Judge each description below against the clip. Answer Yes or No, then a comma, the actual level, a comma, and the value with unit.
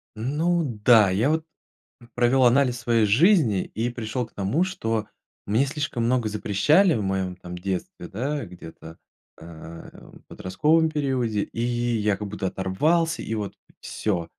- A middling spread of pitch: No, wide, 6.1 semitones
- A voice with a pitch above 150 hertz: No, low, 115 Hz